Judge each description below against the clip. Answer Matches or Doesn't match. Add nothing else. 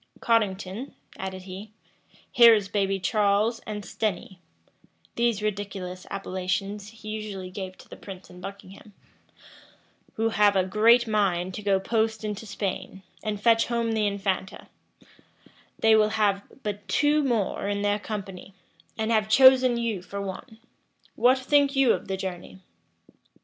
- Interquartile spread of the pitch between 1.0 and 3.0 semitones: Matches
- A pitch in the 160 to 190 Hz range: Doesn't match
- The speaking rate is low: Doesn't match